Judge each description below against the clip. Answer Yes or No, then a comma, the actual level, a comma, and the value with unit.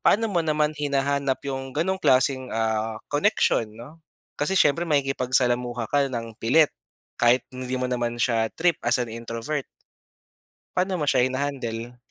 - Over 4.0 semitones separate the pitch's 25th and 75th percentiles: No, average, 3.6 semitones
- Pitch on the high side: No, low, 130 Hz